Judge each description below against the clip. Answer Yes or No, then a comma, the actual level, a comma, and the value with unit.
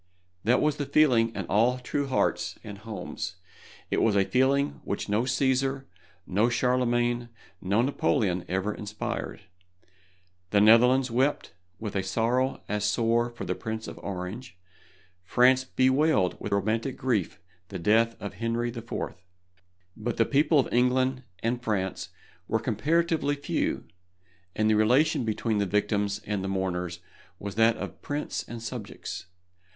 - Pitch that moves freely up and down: No, average, 3.8 semitones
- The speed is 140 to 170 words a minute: Yes, average, 145 wpm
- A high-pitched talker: No, low, 115 Hz